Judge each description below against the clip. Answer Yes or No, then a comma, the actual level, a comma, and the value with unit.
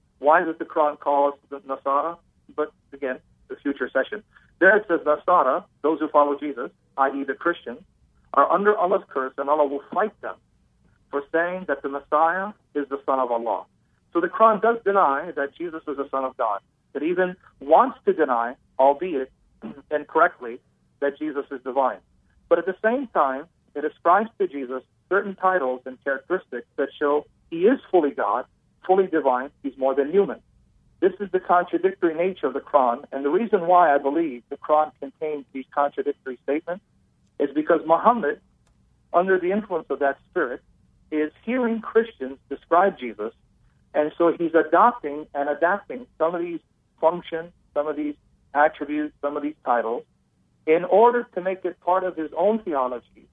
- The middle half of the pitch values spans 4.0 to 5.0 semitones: Yes, average, 4.4 semitones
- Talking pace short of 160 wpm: No, average, 170 wpm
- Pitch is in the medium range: Yes, medium, 150 Hz